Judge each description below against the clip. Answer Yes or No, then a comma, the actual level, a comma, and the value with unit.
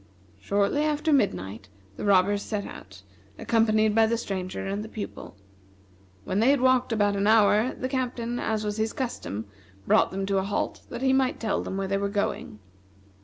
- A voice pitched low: No, high, 210 Hz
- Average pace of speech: Yes, average, 185 wpm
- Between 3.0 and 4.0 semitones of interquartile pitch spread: Yes, average, 3.4 semitones